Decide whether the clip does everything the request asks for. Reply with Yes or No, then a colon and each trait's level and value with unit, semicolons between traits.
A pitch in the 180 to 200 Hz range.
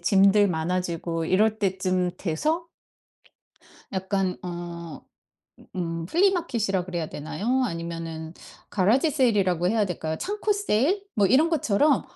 Yes: high, 190 Hz